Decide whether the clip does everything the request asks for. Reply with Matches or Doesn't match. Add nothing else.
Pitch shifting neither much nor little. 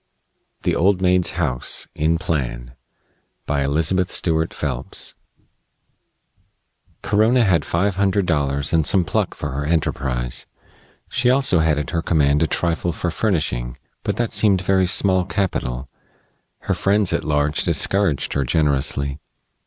Matches